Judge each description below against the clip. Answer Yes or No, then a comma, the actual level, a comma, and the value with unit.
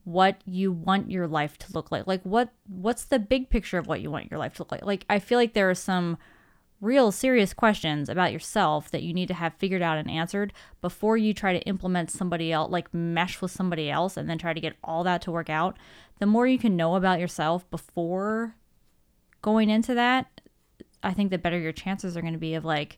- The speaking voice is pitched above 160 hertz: Yes, medium, 185 Hz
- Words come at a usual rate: No, fast, 230 wpm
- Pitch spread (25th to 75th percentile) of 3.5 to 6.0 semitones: Yes, average, 3.8 semitones